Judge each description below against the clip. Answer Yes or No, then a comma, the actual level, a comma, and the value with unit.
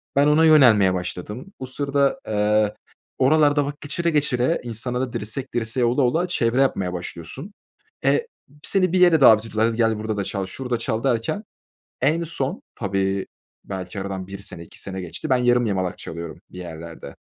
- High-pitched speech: No, low, 115 Hz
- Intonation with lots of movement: Yes, wide, 6.1 semitones